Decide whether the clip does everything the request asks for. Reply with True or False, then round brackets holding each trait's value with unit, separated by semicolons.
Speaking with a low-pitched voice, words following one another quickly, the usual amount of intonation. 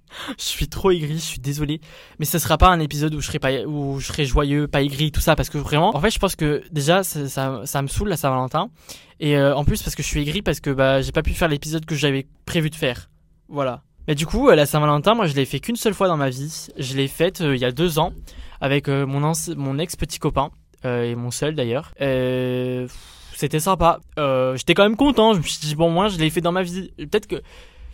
False (150 Hz; 265 wpm; 3.5 semitones)